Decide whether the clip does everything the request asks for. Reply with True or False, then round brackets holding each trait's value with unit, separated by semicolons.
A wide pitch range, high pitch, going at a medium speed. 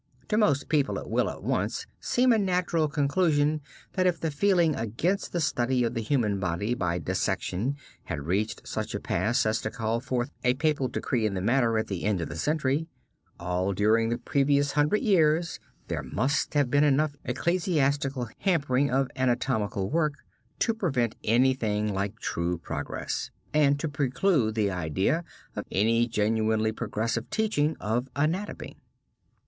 False (5.8 semitones; 130 Hz; 160 wpm)